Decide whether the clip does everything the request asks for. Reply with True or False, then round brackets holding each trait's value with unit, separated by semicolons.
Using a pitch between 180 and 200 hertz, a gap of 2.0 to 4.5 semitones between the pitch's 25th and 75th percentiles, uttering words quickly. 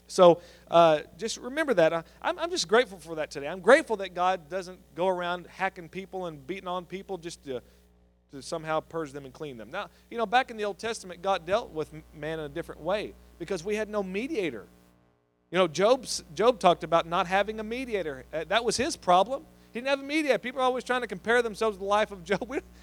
False (185 Hz; 5.3 semitones; 230 wpm)